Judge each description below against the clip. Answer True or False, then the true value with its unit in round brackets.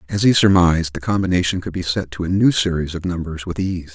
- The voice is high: False (90 Hz)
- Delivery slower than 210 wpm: False (245 wpm)